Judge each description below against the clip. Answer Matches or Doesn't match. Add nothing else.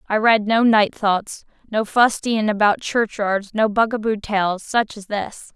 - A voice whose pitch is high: Matches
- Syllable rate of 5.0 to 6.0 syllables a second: Doesn't match